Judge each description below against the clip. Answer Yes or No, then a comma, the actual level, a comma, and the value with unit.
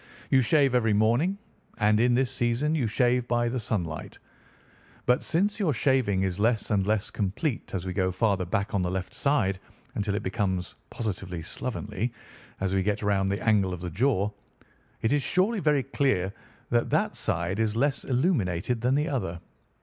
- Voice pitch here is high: No, low, 110 Hz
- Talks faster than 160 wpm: Yes, average, 180 wpm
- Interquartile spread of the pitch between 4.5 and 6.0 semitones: Yes, average, 5.0 semitones